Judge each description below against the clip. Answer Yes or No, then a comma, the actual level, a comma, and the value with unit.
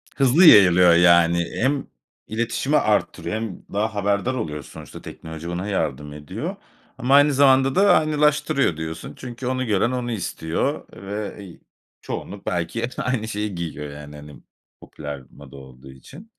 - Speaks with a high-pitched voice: No, low, 100 Hz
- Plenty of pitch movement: Yes, wide, 8.0 semitones